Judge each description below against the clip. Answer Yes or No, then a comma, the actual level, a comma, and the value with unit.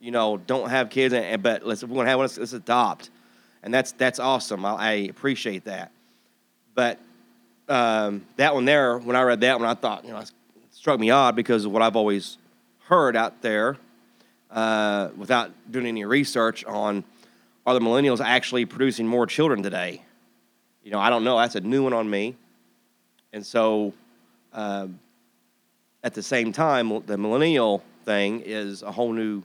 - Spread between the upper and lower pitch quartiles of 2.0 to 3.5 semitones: Yes, average, 2.8 semitones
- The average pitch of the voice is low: Yes, low, 115 Hz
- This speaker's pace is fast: No, average, 175 wpm